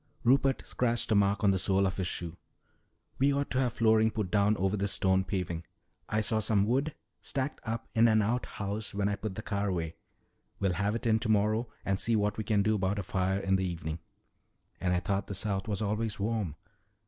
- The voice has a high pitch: No, low, 105 Hz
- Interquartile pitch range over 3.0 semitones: No, narrow, 2.6 semitones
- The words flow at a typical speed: No, fast, 215 wpm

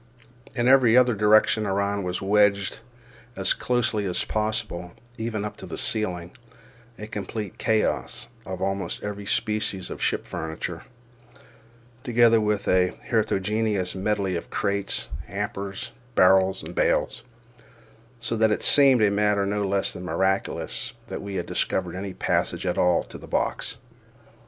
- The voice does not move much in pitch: Yes, narrow, 2.2 semitones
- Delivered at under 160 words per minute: Yes, average, 140 wpm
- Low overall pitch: Yes, low, 100 Hz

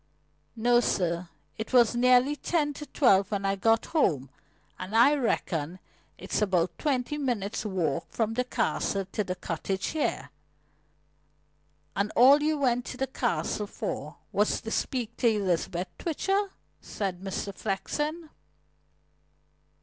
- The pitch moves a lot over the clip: Yes, wide, 5.8 semitones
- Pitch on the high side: Yes, high, 225 Hz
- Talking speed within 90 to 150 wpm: Yes, slow, 135 wpm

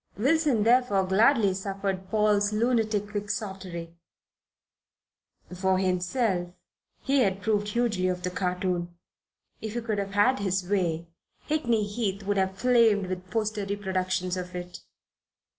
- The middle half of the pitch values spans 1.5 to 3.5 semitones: Yes, average, 2.8 semitones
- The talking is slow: Yes, slow, 125 wpm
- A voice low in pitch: No, high, 200 Hz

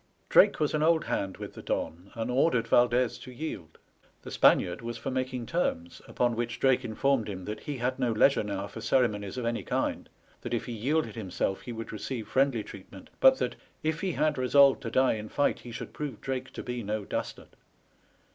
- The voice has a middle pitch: No, low, 120 Hz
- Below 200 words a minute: No, fast, 205 wpm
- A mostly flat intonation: No, average, 3.9 semitones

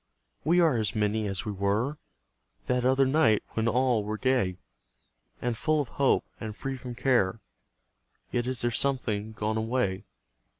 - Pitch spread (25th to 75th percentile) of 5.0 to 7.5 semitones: No, average, 3.6 semitones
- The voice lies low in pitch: Yes, low, 120 Hz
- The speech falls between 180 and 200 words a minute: No, average, 160 wpm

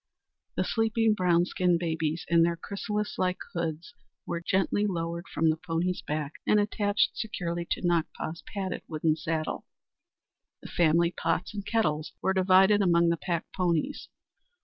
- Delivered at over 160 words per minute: No, average, 150 wpm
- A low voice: No, medium, 175 Hz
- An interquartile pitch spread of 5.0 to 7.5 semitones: No, average, 2.8 semitones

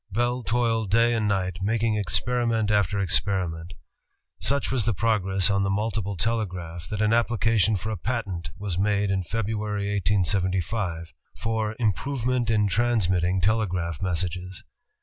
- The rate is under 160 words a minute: Yes, average, 145 wpm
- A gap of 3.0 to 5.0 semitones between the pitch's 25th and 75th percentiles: Yes, average, 3.5 semitones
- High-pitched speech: No, low, 105 Hz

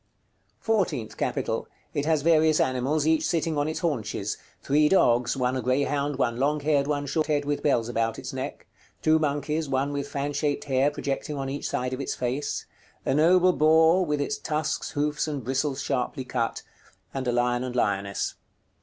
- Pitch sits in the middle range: Yes, medium, 145 Hz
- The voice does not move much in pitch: No, average, 3.1 semitones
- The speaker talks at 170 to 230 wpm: Yes, average, 180 wpm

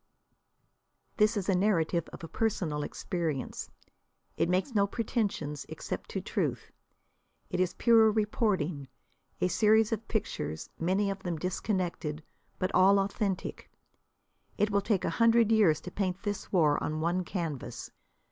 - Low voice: No, high, 190 Hz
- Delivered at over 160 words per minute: No, average, 140 wpm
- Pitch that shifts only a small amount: No, average, 4.1 semitones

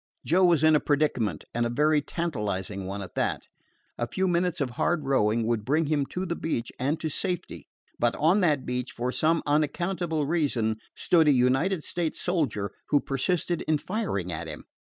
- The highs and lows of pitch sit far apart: Yes, wide, 6.2 semitones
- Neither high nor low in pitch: Yes, medium, 150 Hz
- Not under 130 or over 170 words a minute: No, average, 185 wpm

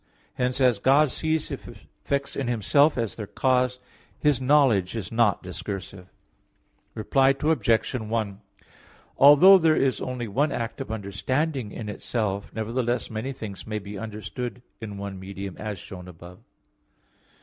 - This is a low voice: Yes, low, 115 Hz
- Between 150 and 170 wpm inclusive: No, average, 140 wpm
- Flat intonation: No, average, 4.8 semitones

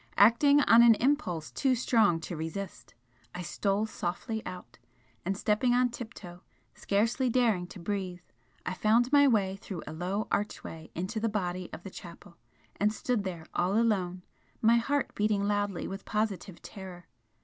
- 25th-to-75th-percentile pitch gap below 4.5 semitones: Yes, average, 4.1 semitones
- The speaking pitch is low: No, high, 205 Hz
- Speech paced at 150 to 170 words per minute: Yes, average, 160 wpm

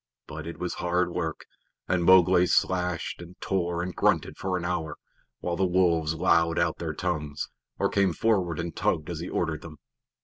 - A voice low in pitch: Yes, very low, 85 Hz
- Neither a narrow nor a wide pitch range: No, narrow, 1.6 semitones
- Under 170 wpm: No, average, 180 wpm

